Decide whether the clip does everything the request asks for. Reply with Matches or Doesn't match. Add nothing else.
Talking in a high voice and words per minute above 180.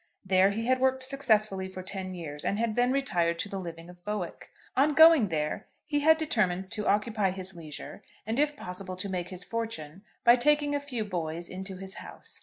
Matches